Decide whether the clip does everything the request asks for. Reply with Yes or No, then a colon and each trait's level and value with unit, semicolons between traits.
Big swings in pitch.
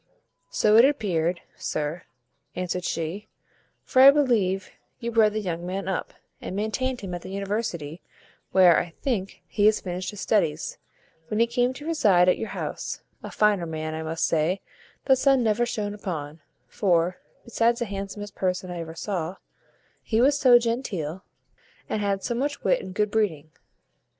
No: average, 4.7 semitones